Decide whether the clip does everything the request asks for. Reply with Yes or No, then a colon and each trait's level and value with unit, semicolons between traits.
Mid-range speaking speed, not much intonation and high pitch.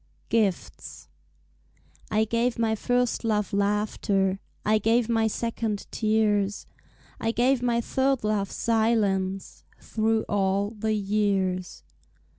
No: slow, 105 wpm; narrow, 2.3 semitones; high, 215 Hz